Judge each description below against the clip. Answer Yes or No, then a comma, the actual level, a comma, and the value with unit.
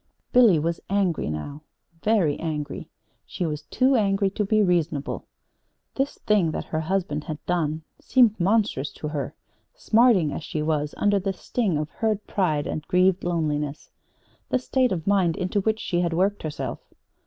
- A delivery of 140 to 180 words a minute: Yes, average, 165 wpm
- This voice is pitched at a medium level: Yes, medium, 180 Hz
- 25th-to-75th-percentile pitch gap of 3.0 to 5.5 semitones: Yes, average, 5.1 semitones